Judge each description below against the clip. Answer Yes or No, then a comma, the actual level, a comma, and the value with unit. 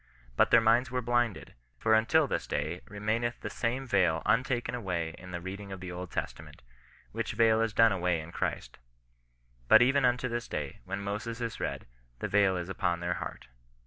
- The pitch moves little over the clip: No, average, 4.7 semitones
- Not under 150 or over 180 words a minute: No, average, 195 wpm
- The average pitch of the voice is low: Yes, low, 105 Hz